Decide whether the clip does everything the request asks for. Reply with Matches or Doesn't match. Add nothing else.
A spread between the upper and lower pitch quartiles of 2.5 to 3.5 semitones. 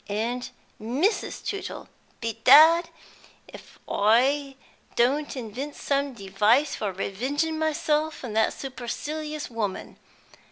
Doesn't match